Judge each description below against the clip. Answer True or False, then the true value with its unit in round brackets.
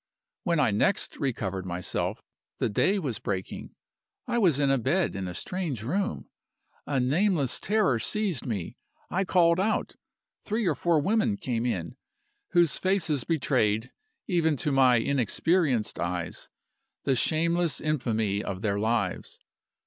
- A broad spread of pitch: True (7.9 semitones)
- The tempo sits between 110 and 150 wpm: True (140 wpm)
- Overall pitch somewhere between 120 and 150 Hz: True (140 Hz)